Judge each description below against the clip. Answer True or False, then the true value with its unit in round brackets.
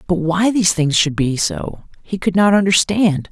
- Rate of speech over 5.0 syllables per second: False (4.6 syllables/s)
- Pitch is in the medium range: True (175 Hz)